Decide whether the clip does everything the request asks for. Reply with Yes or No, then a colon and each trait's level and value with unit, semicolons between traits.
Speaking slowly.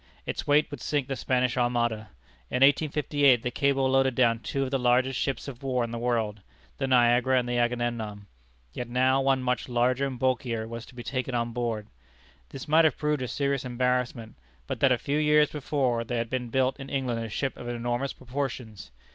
No: fast, 205 wpm